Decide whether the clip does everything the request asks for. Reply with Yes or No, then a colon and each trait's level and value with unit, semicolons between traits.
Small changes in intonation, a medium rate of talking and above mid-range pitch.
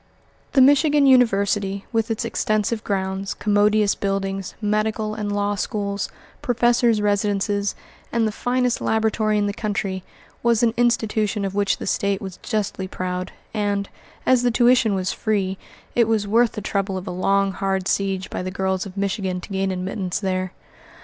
Yes: narrow, 2.3 semitones; average, 165 wpm; high, 205 Hz